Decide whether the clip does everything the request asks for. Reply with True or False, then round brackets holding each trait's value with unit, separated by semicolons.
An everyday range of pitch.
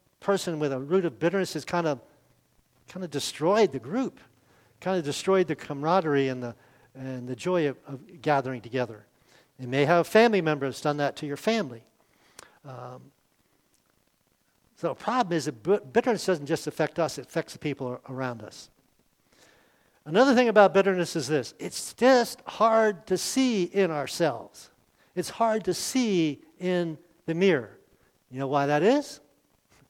False (5.8 semitones)